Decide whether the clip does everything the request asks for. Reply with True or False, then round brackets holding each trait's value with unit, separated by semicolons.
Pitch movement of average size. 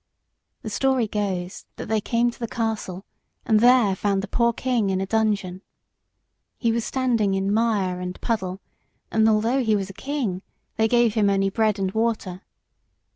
True (3.2 semitones)